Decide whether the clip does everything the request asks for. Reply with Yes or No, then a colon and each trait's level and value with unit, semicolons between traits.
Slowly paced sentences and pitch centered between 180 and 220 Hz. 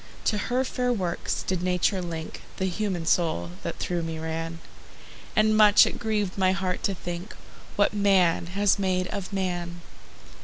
No: average, 160 wpm; medium, 185 Hz